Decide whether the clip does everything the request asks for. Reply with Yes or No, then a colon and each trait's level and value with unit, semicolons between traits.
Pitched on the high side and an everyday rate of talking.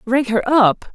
Yes: high, 245 Hz; average, 190 wpm